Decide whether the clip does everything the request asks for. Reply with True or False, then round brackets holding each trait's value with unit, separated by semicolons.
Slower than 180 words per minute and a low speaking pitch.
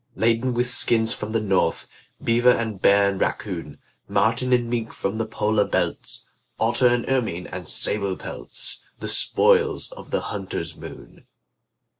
True (150 wpm; 115 Hz)